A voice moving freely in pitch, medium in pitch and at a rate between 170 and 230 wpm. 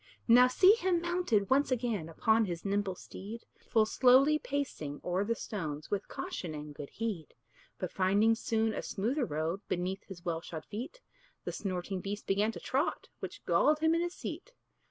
No: wide, 6.1 semitones; high, 210 Hz; average, 175 wpm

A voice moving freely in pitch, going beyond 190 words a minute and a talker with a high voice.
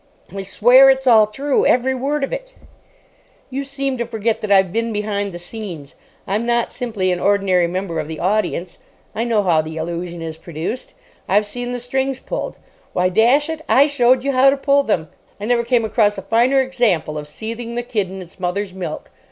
Yes: wide, 5.7 semitones; average, 200 wpm; high, 220 Hz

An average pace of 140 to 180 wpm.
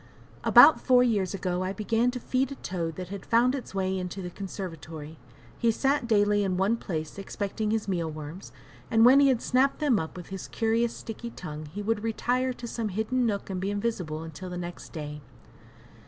No: average, 200 wpm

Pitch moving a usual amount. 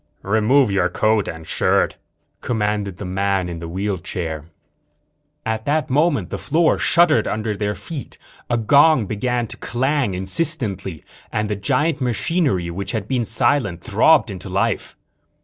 No: wide, 5.7 semitones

